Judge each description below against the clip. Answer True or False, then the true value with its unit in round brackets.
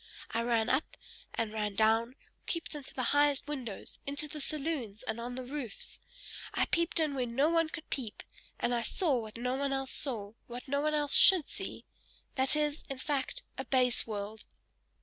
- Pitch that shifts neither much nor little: True (4.2 semitones)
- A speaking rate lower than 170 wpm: False (190 wpm)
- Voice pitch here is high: True (265 Hz)